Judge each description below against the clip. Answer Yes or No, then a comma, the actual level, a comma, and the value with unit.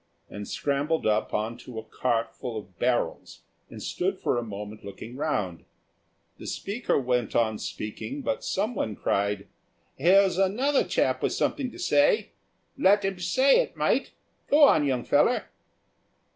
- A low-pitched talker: Yes, low, 130 Hz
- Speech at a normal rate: Yes, average, 150 wpm